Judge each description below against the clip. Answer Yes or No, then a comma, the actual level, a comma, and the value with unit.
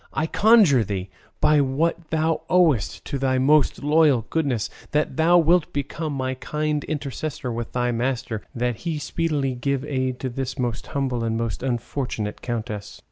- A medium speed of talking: Yes, average, 160 wpm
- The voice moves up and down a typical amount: Yes, average, 3.9 semitones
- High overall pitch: No, low, 135 Hz